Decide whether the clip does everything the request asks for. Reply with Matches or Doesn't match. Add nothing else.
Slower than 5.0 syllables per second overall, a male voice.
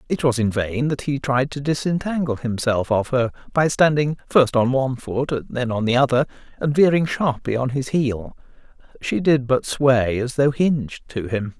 Matches